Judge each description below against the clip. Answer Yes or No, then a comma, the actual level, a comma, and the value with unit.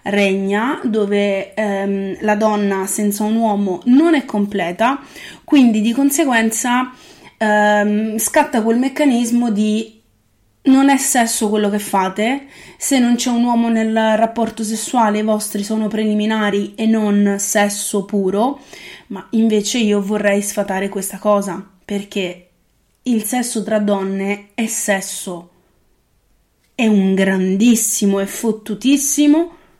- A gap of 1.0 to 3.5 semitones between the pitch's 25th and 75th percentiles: Yes, average, 2.9 semitones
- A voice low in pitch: No, high, 215 Hz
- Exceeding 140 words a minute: No, average, 120 wpm